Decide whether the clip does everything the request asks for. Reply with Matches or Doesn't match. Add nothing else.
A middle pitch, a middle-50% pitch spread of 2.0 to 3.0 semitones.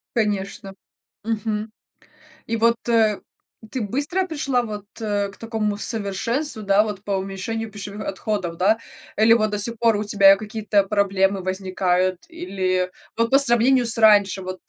Doesn't match